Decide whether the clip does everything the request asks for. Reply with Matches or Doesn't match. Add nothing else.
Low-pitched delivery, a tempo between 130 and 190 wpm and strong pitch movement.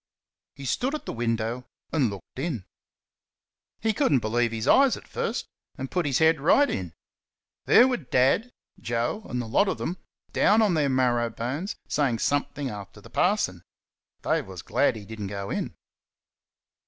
Matches